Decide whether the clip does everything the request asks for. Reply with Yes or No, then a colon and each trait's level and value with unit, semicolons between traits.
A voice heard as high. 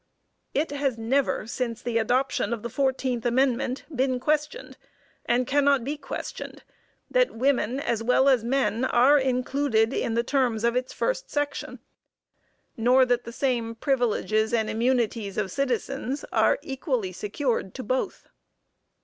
Yes: very high, 250 Hz